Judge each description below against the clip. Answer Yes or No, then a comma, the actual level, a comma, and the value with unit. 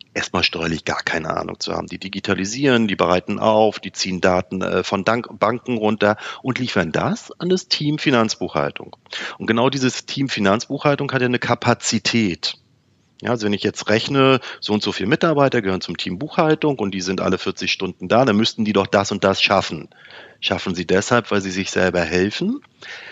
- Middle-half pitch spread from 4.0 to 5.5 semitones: Yes, average, 5.1 semitones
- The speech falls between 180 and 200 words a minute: Yes, average, 185 wpm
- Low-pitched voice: Yes, low, 110 Hz